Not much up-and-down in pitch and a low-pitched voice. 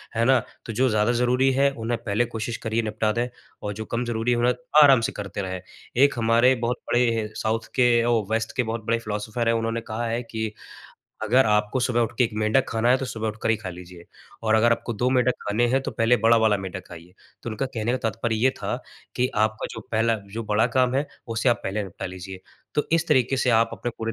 Yes: narrow, 2.1 semitones; low, 115 Hz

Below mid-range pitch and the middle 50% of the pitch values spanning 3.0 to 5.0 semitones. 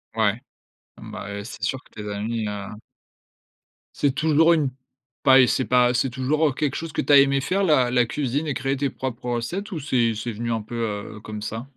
Yes: low, 125 Hz; average, 4.1 semitones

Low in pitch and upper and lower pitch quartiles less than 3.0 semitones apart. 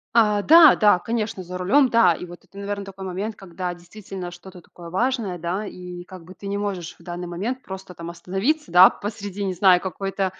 No: high, 190 Hz; narrow, 2.6 semitones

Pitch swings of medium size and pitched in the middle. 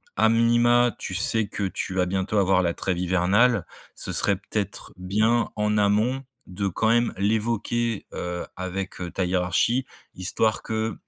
No: average, 3.7 semitones; low, 105 Hz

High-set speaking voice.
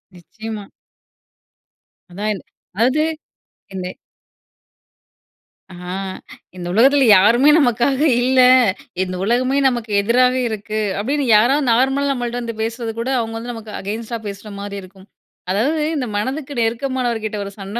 Yes: high, 230 Hz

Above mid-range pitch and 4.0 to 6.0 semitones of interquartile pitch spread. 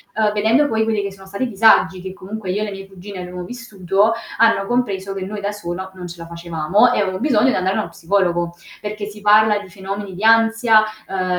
No: high, 200 Hz; average, 2.7 semitones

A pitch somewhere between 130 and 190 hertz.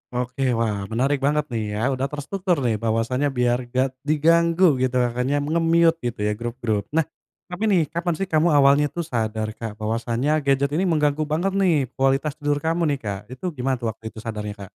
Yes: low, 135 Hz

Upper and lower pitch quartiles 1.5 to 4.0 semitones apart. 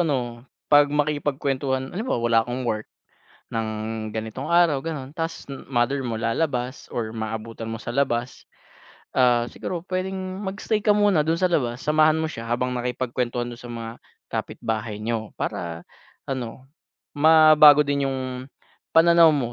No: average, 4.7 semitones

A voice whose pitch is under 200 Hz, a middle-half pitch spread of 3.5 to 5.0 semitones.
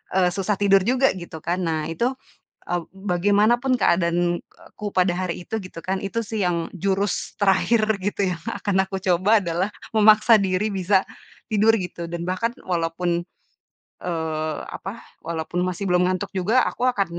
No: high, 190 Hz; average, 3.0 semitones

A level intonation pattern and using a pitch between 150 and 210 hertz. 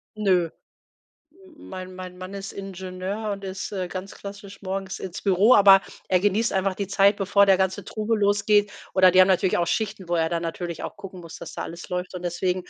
Yes: narrow, 1.7 semitones; high, 190 Hz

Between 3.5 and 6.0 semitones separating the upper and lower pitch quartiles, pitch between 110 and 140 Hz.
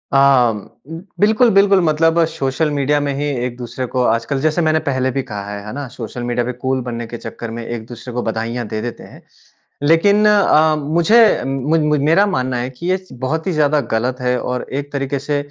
Yes: average, 4.4 semitones; low, 135 Hz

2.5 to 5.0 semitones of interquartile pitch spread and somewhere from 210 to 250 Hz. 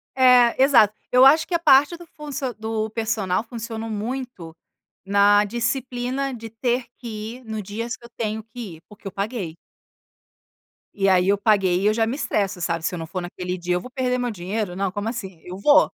Yes: average, 4.2 semitones; high, 220 Hz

